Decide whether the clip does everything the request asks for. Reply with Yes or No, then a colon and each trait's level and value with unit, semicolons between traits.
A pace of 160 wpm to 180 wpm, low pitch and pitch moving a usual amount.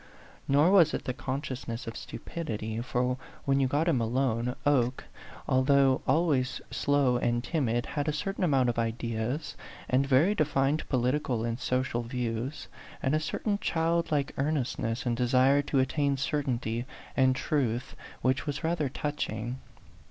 No: average, 145 wpm; low, 130 Hz; average, 3.3 semitones